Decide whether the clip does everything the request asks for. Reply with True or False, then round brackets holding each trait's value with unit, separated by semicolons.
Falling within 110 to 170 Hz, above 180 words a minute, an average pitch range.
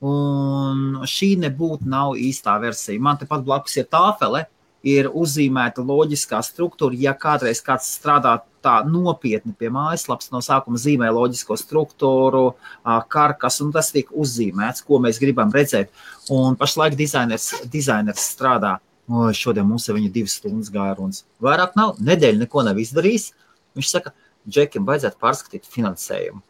False (140 Hz; 145 wpm; 3.6 semitones)